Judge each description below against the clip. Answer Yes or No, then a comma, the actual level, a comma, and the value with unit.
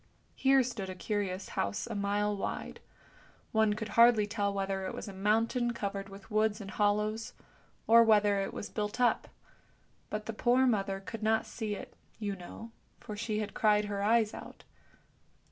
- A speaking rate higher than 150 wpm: Yes, average, 175 wpm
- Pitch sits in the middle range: No, high, 210 Hz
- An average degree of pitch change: No, narrow, 1.8 semitones